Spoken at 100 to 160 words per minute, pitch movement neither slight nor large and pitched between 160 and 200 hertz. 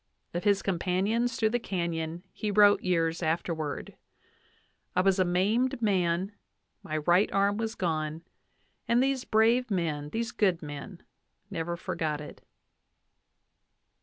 Yes: slow, 135 wpm; average, 4.6 semitones; medium, 185 Hz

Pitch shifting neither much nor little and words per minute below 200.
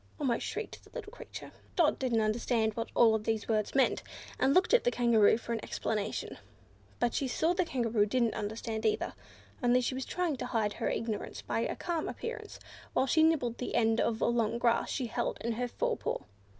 No: average, 3.1 semitones; fast, 205 wpm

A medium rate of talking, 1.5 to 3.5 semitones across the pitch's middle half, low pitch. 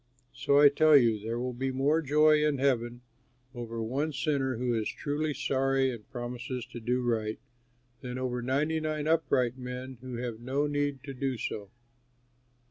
Yes: average, 170 wpm; average, 2.9 semitones; low, 130 Hz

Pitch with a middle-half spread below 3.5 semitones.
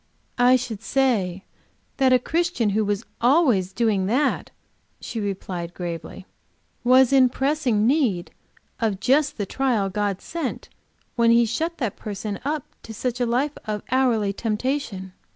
No: average, 4.6 semitones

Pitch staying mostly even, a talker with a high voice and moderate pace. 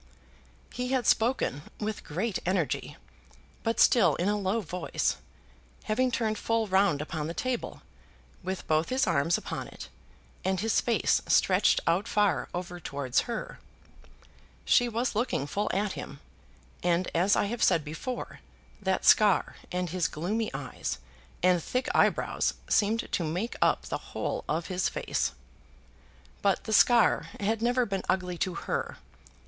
No: average, 4.6 semitones; high, 195 Hz; average, 150 wpm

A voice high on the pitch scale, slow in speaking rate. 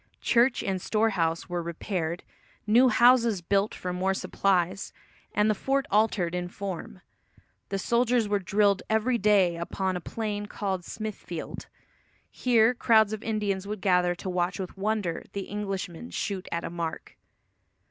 No: high, 200 Hz; average, 145 wpm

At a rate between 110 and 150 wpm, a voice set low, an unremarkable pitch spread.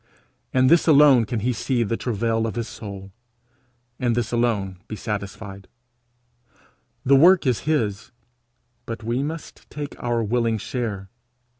Yes: average, 145 wpm; low, 115 Hz; average, 3.5 semitones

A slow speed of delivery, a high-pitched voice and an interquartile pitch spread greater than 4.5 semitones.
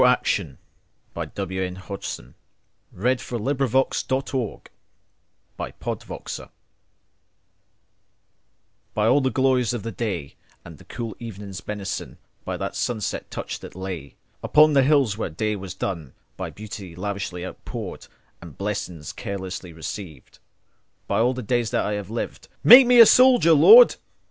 No: slow, 120 wpm; low, 105 Hz; wide, 5.6 semitones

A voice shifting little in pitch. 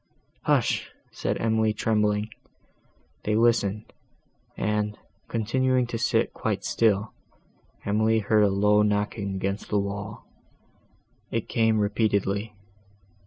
Yes: narrow, 1.4 semitones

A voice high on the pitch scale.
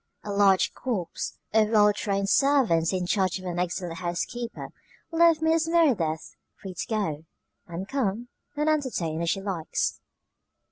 Yes: high, 200 Hz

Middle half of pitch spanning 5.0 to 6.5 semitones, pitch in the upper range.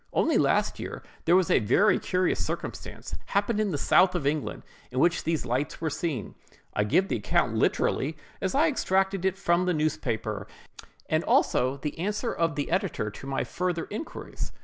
No: wide, 5.4 semitones; medium, 170 Hz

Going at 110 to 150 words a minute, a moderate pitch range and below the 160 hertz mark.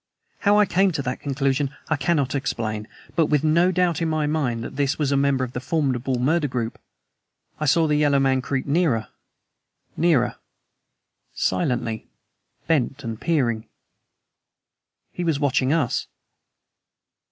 Yes: average, 145 wpm; average, 3.7 semitones; medium, 140 Hz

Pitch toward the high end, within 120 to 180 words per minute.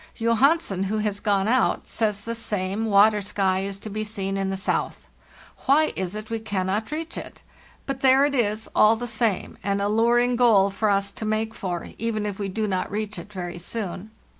No: high, 215 Hz; average, 200 wpm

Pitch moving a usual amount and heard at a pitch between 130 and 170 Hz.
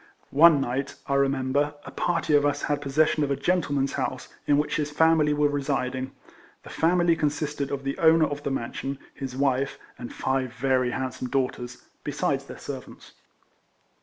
No: narrow, 1.9 semitones; medium, 140 Hz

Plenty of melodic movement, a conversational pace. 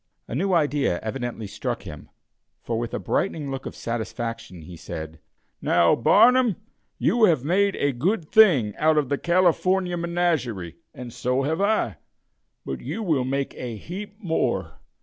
Yes: wide, 7.5 semitones; average, 155 wpm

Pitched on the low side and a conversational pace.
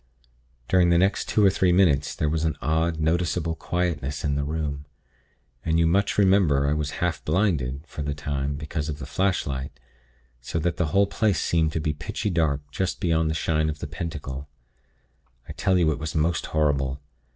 Yes: very low, 80 Hz; average, 190 wpm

